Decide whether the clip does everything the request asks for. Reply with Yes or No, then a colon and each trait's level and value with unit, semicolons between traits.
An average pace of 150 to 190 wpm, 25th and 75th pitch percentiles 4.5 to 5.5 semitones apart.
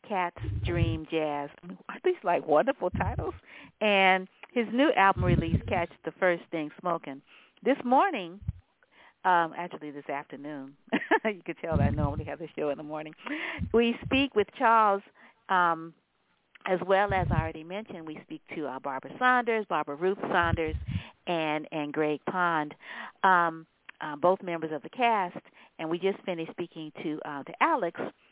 Yes: average, 160 wpm; average, 4.9 semitones